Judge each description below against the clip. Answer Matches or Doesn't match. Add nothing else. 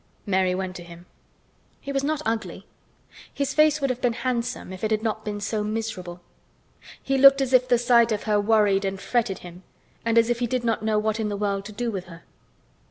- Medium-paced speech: Doesn't match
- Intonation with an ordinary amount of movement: Matches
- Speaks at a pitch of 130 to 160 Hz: Doesn't match